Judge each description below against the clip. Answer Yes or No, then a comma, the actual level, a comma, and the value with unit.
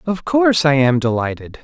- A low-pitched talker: No, medium, 155 Hz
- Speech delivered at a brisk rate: No, average, 185 wpm